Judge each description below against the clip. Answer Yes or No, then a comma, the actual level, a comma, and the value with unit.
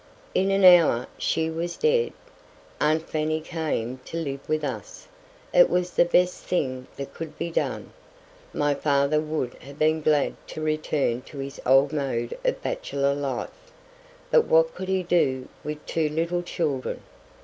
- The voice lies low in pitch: No, medium, 155 Hz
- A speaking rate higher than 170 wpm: No, average, 160 wpm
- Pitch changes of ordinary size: Yes, average, 3.8 semitones